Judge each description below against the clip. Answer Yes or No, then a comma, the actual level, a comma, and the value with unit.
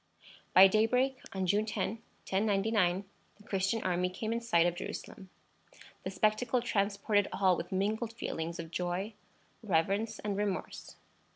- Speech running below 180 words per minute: Yes, slow, 135 wpm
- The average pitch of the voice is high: Yes, high, 200 Hz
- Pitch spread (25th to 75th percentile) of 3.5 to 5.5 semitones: No, average, 2.9 semitones